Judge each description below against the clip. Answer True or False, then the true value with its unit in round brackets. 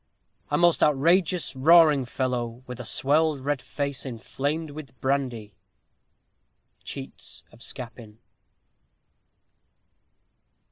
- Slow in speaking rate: True (95 wpm)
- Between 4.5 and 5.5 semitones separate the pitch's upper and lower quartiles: False (3.8 semitones)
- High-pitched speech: False (135 Hz)